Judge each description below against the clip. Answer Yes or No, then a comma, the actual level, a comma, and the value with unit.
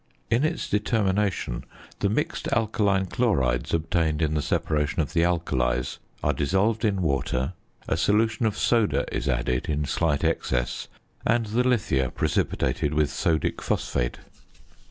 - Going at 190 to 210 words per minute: No, slow, 135 wpm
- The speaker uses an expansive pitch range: Yes, wide, 7.1 semitones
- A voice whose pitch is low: Yes, very low, 85 Hz